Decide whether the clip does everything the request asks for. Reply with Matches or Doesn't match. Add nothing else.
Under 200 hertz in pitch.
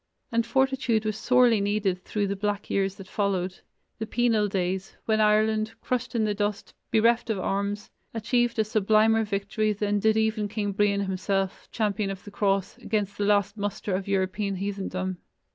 Doesn't match